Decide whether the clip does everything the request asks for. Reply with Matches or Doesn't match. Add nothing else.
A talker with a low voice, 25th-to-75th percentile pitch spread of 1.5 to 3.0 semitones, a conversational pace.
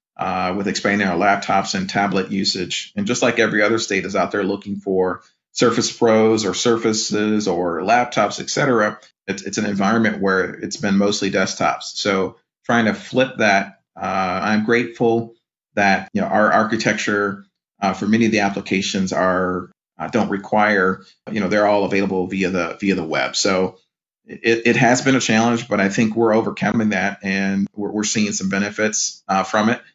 Matches